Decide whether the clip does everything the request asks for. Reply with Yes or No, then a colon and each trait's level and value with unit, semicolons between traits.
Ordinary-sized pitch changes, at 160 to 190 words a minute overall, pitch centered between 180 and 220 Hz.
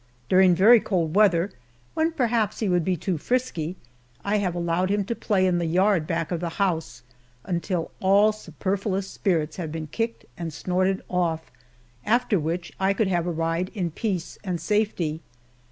Yes: average, 3.4 semitones; average, 170 wpm; medium, 185 Hz